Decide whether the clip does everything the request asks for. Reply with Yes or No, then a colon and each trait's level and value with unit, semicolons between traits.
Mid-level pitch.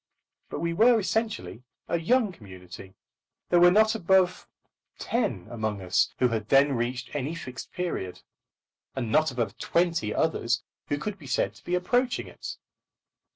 Yes: medium, 155 Hz